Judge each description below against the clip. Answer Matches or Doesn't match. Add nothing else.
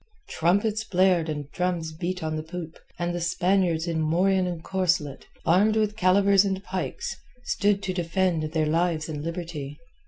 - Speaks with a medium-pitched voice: Matches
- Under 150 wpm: Doesn't match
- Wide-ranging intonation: Doesn't match